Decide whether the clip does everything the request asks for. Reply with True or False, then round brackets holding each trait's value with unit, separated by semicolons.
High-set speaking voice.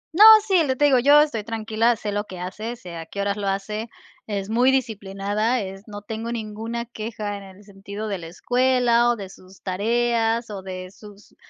True (215 Hz)